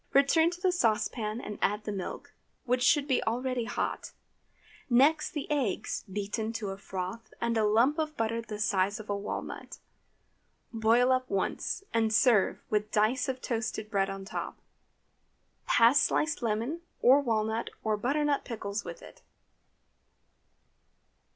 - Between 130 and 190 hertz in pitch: No, high, 230 Hz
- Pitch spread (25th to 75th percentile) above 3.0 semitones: Yes, average, 3.7 semitones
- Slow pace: No, average, 150 wpm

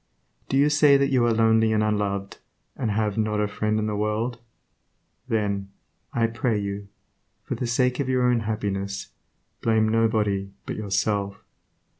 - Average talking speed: Yes, average, 160 wpm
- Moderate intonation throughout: No, narrow, 2.3 semitones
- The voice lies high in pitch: No, low, 110 Hz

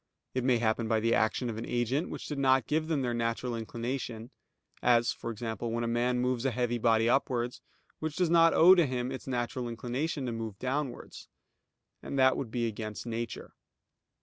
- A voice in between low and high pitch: No, low, 120 Hz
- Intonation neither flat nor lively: No, narrow, 2.2 semitones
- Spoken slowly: No, average, 195 wpm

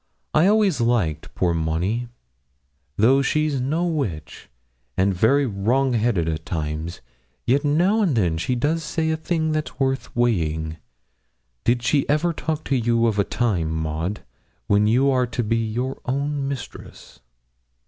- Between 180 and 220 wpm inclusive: No, average, 155 wpm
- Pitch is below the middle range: Yes, low, 120 Hz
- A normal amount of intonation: No, wide, 6.8 semitones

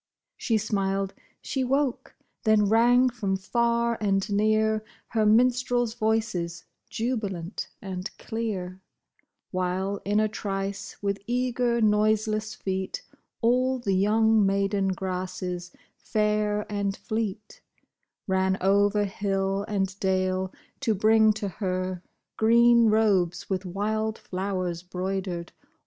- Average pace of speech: No, slow, 110 wpm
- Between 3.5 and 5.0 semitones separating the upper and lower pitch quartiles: No, average, 2.7 semitones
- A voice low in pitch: No, high, 205 Hz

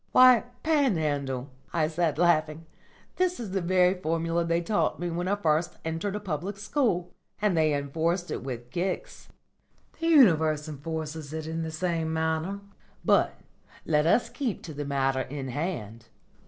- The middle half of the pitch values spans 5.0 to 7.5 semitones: No, average, 3.6 semitones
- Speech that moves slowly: No, average, 160 wpm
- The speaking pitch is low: No, medium, 165 Hz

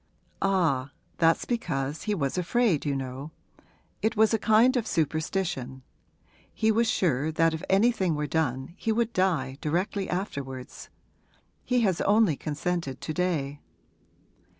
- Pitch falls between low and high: Yes, medium, 165 Hz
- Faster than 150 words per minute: No, slow, 135 wpm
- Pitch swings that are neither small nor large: No, wide, 6.8 semitones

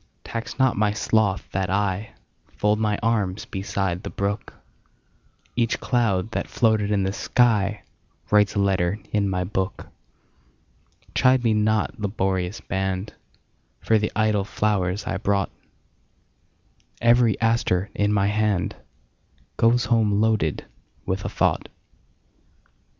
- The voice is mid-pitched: No, low, 105 Hz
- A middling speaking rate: No, slow, 105 wpm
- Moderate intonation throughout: No, narrow, 2.3 semitones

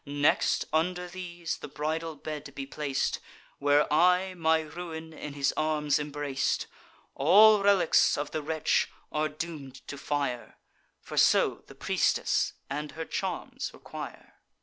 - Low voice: No, medium, 155 Hz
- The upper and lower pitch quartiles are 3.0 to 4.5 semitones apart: No, narrow, 2.6 semitones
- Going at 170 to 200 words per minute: No, slow, 135 wpm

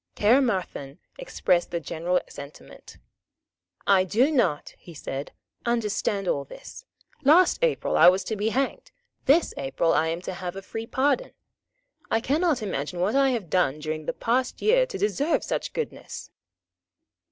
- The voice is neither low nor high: No, high, 205 Hz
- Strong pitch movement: Yes, wide, 7.8 semitones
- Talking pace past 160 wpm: No, average, 150 wpm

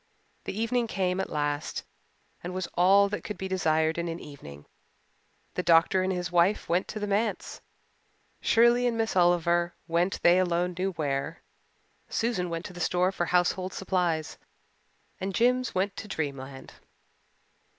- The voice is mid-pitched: Yes, medium, 180 Hz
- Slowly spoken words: No, average, 155 wpm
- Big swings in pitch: No, narrow, 2.5 semitones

